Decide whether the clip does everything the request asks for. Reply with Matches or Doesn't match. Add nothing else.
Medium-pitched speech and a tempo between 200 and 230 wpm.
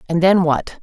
Matches